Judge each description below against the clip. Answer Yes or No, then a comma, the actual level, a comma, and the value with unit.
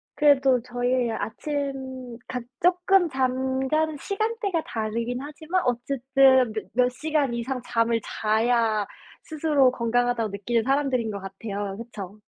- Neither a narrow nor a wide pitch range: Yes, average, 3.7 semitones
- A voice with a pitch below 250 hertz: No, very high, 255 Hz